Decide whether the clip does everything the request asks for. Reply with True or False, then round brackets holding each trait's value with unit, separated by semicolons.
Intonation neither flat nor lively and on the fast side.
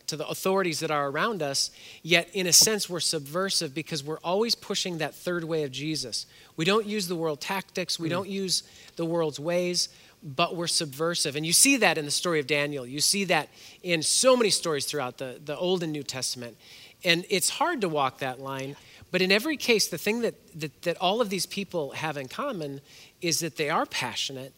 True (3.9 semitones; 215 wpm)